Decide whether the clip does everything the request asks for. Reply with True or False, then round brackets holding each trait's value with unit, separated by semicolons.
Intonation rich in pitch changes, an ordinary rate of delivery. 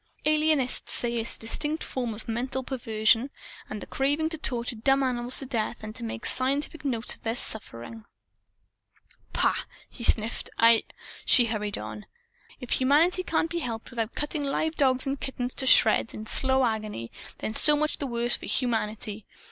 False (3.8 semitones; 170 wpm)